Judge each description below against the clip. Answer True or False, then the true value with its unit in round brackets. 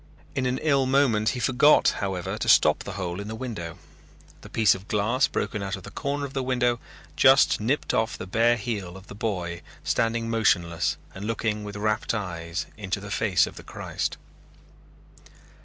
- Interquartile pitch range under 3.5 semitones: False (4.2 semitones)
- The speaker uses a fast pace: False (185 wpm)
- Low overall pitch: True (110 Hz)